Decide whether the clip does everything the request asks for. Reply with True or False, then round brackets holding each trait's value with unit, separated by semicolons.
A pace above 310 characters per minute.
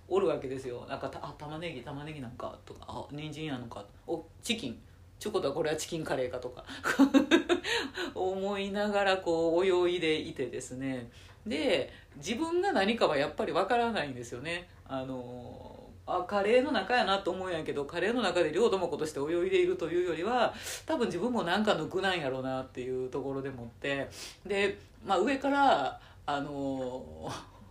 True (355 characters per minute)